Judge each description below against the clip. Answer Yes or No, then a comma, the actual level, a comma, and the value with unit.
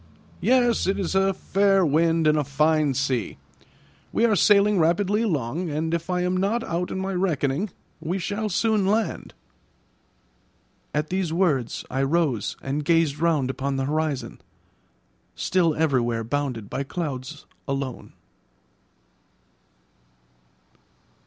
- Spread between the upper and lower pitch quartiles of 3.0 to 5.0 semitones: No, wide, 5.6 semitones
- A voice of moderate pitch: Yes, medium, 165 Hz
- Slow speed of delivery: Yes, slow, 125 wpm